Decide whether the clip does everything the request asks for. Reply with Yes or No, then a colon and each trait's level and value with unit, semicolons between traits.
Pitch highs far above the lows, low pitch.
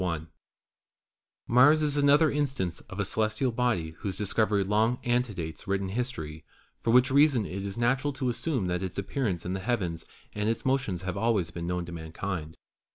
Yes: wide, 5.8 semitones; low, 105 Hz